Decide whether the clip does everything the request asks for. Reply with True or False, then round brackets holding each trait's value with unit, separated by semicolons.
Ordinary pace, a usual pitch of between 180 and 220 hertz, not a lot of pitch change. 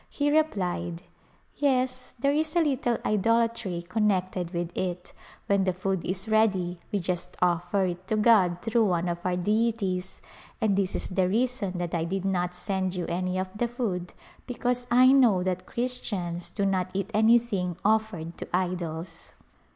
False (170 wpm; 190 Hz; 4.3 semitones)